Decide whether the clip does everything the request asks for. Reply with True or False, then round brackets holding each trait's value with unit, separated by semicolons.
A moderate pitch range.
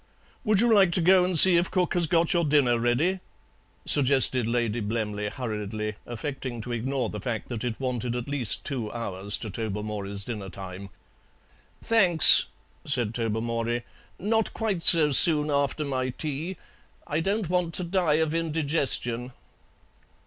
False (6.4 semitones)